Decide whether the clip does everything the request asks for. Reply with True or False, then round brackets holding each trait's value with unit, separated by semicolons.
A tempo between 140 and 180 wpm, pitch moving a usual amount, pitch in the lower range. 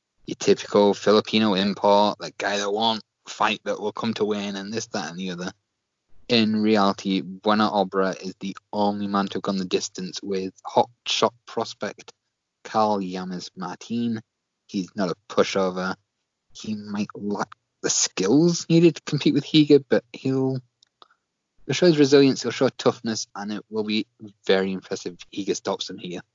True (170 wpm; 3.0 semitones; 105 Hz)